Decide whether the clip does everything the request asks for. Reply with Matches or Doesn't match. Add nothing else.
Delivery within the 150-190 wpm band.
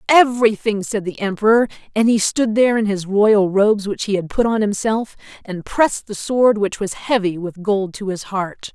Doesn't match